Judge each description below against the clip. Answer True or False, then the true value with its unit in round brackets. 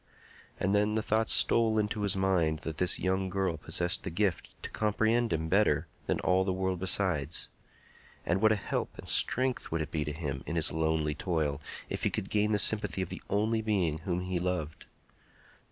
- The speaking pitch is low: True (95 Hz)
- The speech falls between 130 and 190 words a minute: False (200 wpm)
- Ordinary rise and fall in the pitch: True (4.5 semitones)